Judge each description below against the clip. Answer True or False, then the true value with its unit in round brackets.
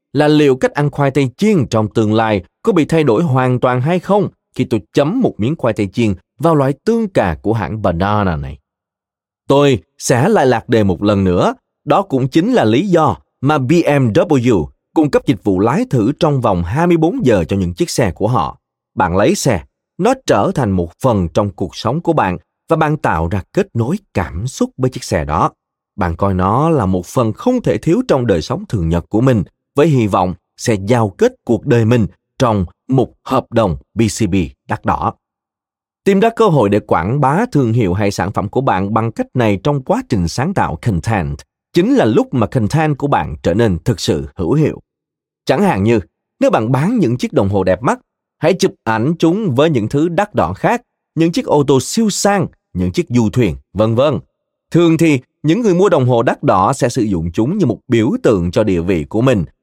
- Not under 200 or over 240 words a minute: True (215 wpm)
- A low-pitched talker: True (120 Hz)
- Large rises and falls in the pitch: True (7.3 semitones)